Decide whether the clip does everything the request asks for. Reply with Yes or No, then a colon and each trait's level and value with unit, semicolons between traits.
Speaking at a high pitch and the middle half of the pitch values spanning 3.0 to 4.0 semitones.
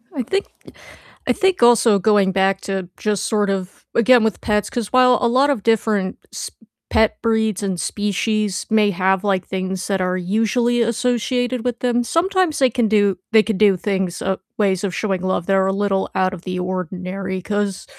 Yes: high, 205 Hz; average, 3.5 semitones